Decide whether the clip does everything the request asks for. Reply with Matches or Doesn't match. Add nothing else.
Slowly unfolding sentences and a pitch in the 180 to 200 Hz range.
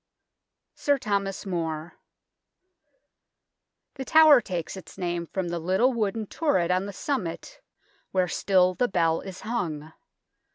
Matches